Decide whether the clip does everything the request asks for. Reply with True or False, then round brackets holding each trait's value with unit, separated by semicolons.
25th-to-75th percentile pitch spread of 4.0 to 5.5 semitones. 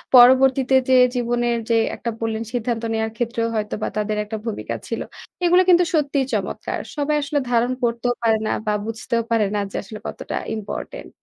False (2.8 semitones)